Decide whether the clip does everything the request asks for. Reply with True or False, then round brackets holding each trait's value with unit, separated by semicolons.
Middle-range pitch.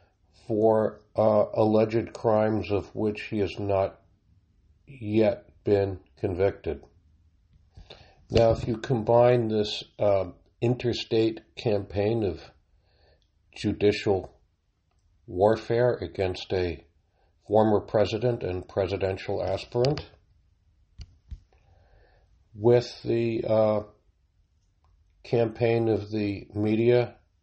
False (100 Hz)